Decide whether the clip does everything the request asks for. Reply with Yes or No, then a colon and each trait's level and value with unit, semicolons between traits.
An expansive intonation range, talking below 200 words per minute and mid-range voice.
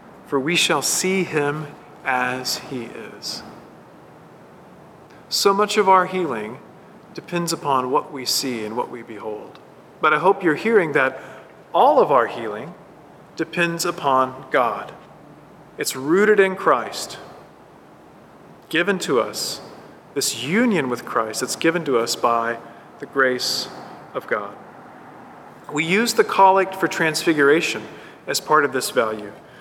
Yes: wide, 6.2 semitones; slow, 135 wpm; medium, 165 Hz